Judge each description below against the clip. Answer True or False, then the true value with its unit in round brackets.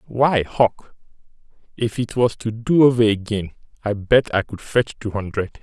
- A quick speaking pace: False (170 wpm)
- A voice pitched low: True (110 Hz)